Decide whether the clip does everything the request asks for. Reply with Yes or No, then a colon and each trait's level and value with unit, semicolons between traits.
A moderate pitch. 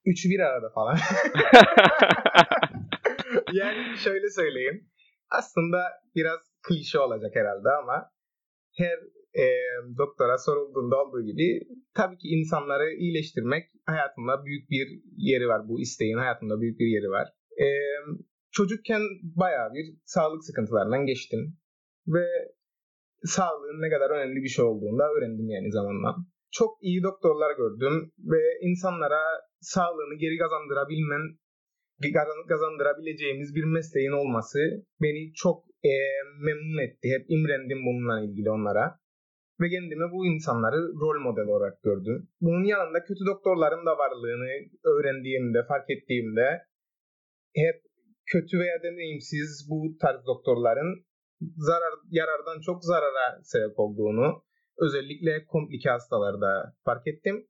Yes: medium, 160 Hz